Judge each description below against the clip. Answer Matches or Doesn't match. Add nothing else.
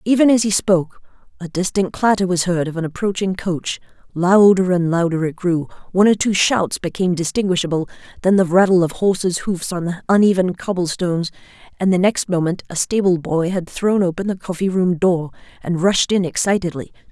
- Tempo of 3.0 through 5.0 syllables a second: Doesn't match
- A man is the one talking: Doesn't match